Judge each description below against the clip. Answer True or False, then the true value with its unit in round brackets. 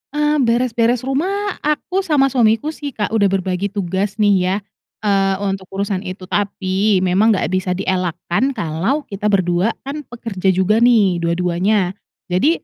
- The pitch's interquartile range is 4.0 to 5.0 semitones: True (4.7 semitones)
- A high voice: True (205 Hz)